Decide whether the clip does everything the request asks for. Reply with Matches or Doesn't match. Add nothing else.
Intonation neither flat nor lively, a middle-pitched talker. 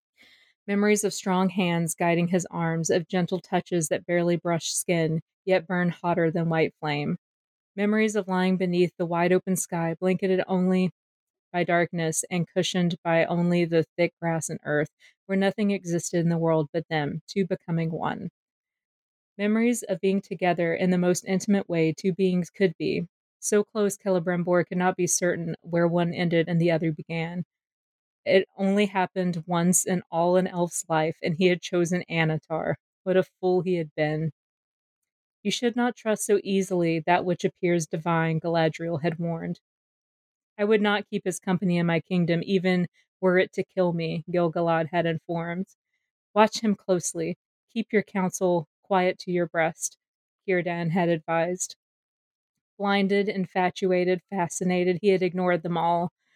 Doesn't match